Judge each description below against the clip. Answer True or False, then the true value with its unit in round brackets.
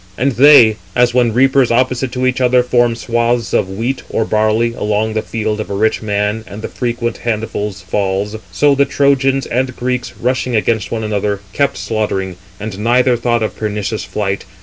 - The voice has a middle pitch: False (115 Hz)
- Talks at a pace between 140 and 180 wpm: True (170 wpm)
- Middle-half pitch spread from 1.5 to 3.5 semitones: True (3.0 semitones)